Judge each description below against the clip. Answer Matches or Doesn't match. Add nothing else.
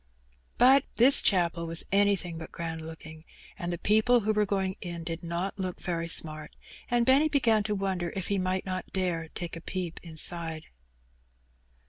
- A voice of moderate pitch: Matches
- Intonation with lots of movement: Doesn't match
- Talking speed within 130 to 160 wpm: Doesn't match